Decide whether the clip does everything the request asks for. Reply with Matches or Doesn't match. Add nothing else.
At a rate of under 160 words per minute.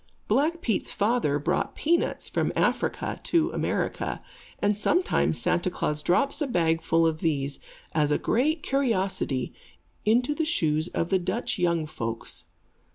Matches